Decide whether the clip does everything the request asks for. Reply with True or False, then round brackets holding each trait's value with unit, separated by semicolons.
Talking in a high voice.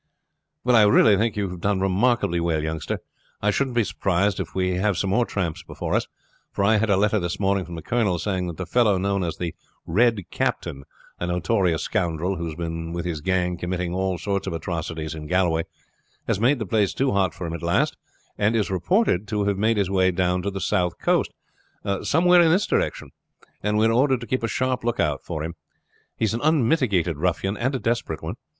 False (95 Hz)